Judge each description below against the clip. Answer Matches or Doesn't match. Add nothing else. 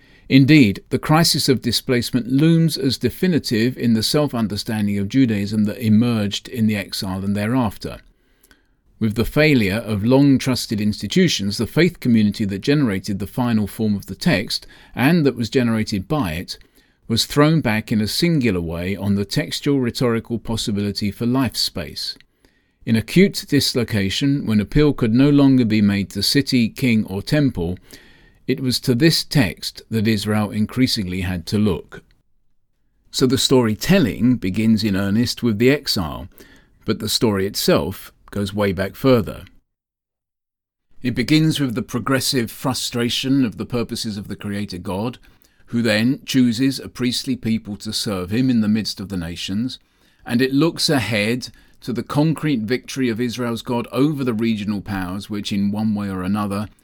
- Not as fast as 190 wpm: Matches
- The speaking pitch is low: Matches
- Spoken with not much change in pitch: Doesn't match